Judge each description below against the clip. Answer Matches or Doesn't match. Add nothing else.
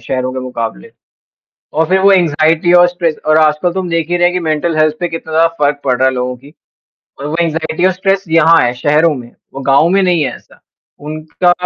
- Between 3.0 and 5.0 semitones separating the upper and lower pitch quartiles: Matches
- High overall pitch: Doesn't match